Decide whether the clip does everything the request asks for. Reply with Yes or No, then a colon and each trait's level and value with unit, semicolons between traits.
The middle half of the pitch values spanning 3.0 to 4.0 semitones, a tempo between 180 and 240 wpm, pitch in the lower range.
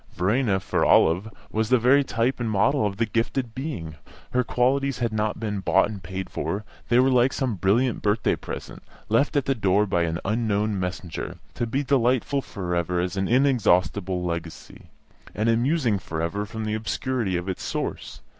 No: average, 4.8 semitones; average, 185 wpm; low, 110 Hz